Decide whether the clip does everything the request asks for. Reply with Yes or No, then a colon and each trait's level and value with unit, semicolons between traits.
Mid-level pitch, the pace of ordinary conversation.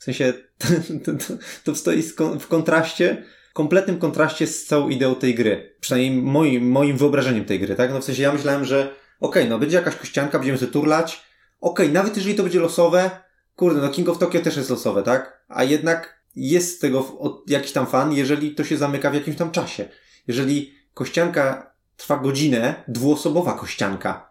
No: medium, 150 Hz; fast, 190 wpm